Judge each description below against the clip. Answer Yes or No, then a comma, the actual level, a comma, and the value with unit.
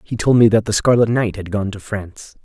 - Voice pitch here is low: Yes, low, 105 Hz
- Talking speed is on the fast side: Yes, fast, 270 wpm